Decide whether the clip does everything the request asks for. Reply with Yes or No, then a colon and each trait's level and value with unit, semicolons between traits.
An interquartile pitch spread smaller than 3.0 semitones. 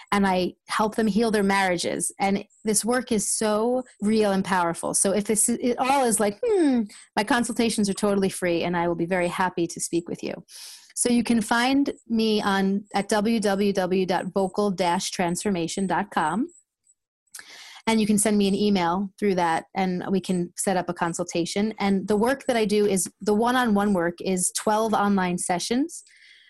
No: average, 3.4 semitones